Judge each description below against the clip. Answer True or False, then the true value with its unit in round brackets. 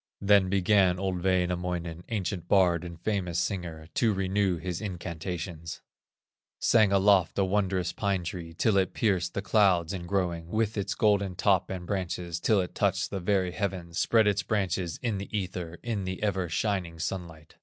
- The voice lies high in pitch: False (95 Hz)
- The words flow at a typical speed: True (165 wpm)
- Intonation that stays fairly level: True (2.3 semitones)